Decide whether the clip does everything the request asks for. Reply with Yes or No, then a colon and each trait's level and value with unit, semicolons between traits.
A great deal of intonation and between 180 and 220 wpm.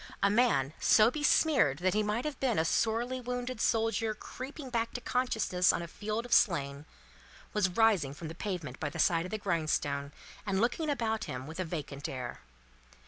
Yes: wide, 6.8 semitones; average, 190 wpm